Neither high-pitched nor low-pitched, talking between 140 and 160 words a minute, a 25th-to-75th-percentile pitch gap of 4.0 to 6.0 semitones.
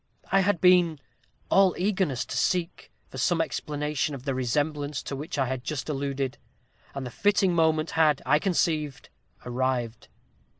Yes: medium, 150 Hz; average, 155 wpm; average, 4.3 semitones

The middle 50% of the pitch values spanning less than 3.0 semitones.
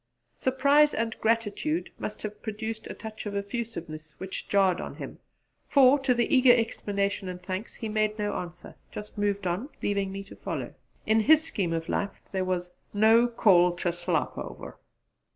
No: average, 3.7 semitones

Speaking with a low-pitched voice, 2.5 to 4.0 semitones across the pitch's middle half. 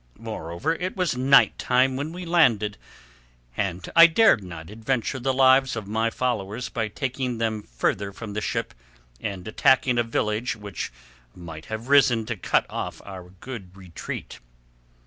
No: low, 115 Hz; average, 4.8 semitones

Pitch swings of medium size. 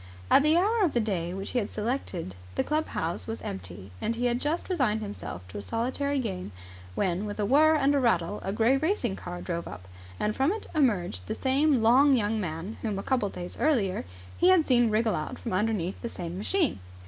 No: wide, 7.0 semitones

